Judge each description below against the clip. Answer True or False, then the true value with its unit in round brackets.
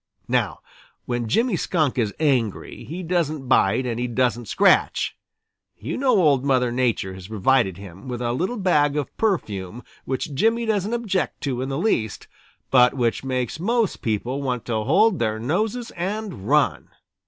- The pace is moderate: True (165 wpm)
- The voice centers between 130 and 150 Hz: True (135 Hz)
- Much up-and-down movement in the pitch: True (7.5 semitones)